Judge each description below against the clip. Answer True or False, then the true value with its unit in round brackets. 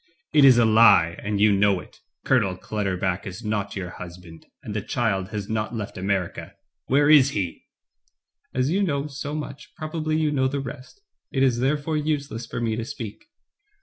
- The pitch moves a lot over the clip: True (6.0 semitones)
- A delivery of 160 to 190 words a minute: True (185 wpm)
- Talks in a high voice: False (115 Hz)